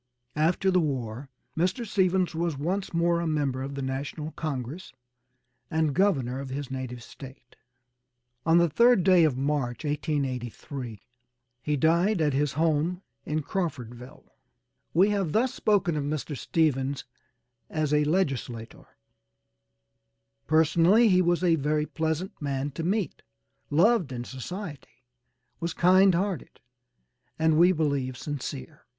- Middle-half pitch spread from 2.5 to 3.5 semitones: No, average, 4.4 semitones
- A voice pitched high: No, medium, 155 Hz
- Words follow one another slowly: Yes, slow, 130 wpm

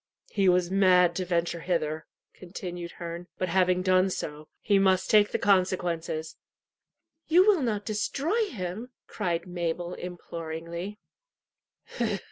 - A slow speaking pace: Yes, slow, 120 wpm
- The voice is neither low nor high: Yes, medium, 180 Hz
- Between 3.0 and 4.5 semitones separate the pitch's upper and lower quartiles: No, narrow, 2.5 semitones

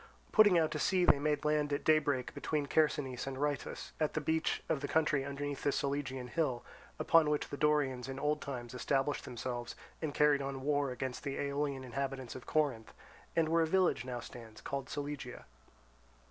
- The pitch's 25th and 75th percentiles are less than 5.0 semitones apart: Yes, narrow, 2.4 semitones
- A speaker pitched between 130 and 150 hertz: Yes, medium, 140 Hz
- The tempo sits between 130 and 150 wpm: No, average, 185 wpm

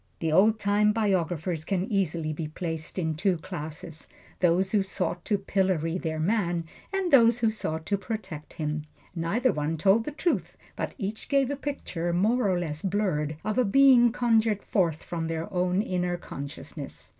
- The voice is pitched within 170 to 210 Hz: Yes, medium, 185 Hz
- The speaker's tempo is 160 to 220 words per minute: Yes, average, 170 wpm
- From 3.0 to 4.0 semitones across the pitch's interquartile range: No, average, 4.9 semitones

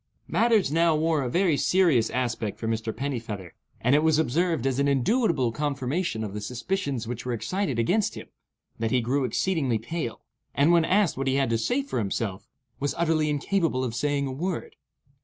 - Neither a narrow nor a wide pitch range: No, wide, 5.8 semitones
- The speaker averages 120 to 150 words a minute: No, average, 190 wpm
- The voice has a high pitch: No, medium, 140 Hz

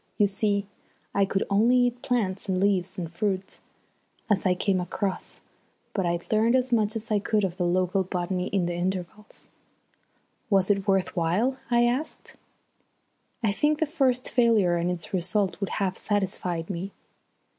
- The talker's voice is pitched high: Yes, high, 195 Hz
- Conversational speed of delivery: Yes, average, 165 wpm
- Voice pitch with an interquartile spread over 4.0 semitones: No, average, 3.2 semitones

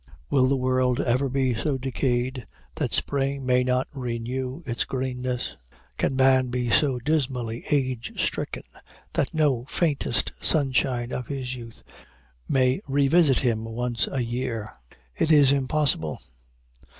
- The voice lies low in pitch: Yes, low, 130 Hz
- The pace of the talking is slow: Yes, slow, 130 wpm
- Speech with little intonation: Yes, narrow, 1.9 semitones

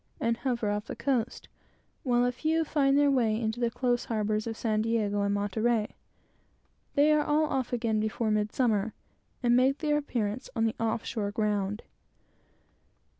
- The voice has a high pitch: Yes, high, 230 Hz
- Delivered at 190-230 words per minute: No, average, 165 wpm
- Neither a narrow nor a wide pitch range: Yes, average, 3.2 semitones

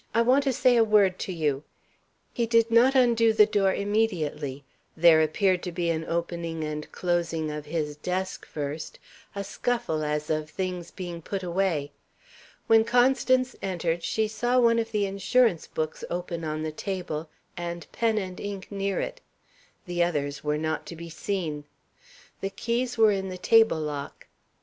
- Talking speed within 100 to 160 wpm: No, average, 170 wpm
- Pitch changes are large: Yes, wide, 5.7 semitones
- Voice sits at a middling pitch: Yes, medium, 180 Hz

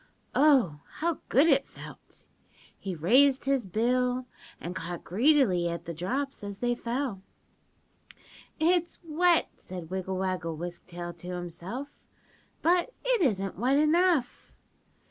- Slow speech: Yes, slow, 125 wpm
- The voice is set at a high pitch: Yes, high, 240 Hz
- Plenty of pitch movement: Yes, wide, 8.1 semitones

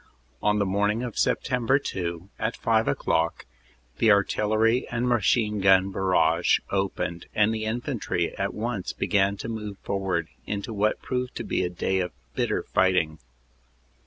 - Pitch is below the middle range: Yes, low, 100 Hz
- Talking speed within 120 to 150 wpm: No, average, 160 wpm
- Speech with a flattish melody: No, average, 3.1 semitones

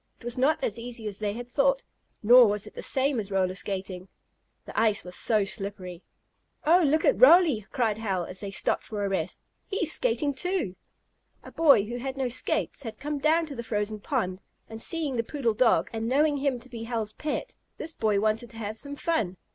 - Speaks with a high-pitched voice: Yes, high, 230 Hz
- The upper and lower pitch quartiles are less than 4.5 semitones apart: No, wide, 5.4 semitones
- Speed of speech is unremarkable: No, fast, 215 wpm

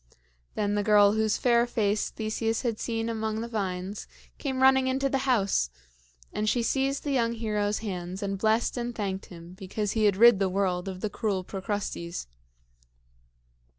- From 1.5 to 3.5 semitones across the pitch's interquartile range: Yes, average, 3.1 semitones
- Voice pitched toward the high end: Yes, high, 215 Hz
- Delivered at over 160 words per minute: Yes, average, 170 wpm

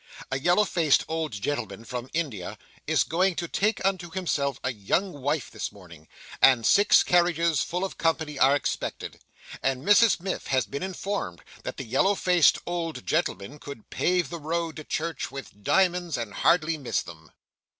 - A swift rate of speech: No, average, 170 wpm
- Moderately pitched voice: Yes, medium, 160 Hz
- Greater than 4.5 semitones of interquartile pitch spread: Yes, average, 5.1 semitones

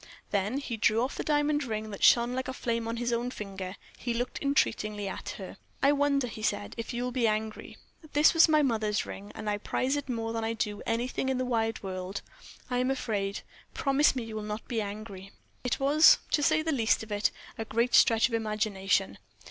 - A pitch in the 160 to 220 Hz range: No, high, 230 Hz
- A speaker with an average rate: No, fast, 215 wpm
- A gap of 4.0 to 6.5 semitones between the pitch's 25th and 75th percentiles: No, average, 3.3 semitones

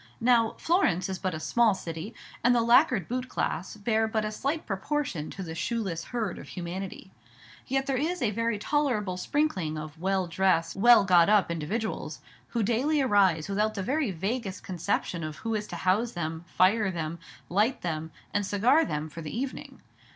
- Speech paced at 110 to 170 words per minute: No, average, 180 wpm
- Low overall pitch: No, high, 205 Hz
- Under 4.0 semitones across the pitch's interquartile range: No, wide, 5.4 semitones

